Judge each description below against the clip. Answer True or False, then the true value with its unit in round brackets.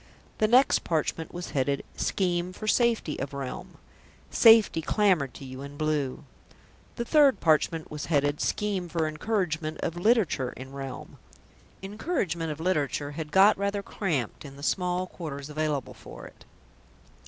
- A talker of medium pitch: True (160 Hz)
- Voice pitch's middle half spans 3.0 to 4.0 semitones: False (5.6 semitones)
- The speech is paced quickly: False (145 wpm)